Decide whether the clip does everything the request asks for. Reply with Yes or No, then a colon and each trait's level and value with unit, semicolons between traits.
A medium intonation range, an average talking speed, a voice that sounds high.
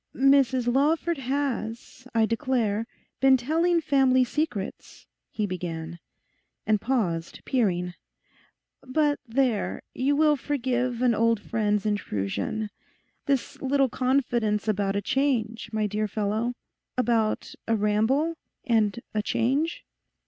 No: average, 4.2 semitones; slow, 105 wpm; high, 235 Hz